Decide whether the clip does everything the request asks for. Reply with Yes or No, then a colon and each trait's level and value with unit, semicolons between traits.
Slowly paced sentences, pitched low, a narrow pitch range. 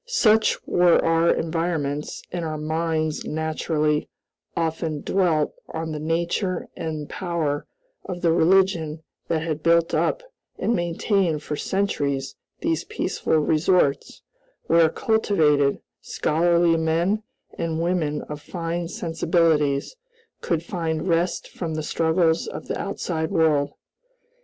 No: slow, 120 wpm; medium, 165 Hz; narrow, 1.9 semitones